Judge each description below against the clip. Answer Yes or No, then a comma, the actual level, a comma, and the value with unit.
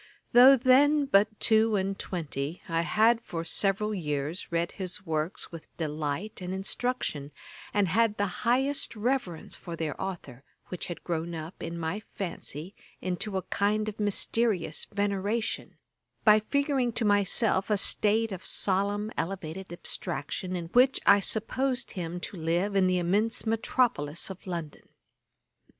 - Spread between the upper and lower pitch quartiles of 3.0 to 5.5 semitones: Yes, average, 4.3 semitones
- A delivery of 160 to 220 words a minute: No, average, 145 wpm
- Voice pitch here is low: No, high, 195 Hz